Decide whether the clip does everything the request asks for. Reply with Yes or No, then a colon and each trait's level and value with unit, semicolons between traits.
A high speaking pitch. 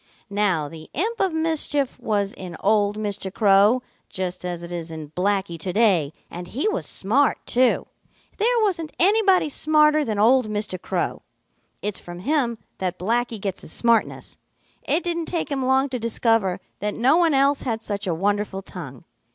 Yes: high, 215 Hz